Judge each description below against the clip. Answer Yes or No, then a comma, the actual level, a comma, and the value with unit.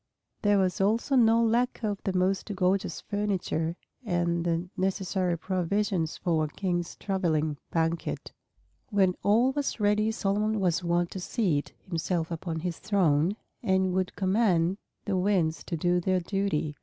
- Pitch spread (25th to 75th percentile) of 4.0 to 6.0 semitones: No, average, 3.1 semitones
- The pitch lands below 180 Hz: No, medium, 185 Hz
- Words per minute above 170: No, average, 145 wpm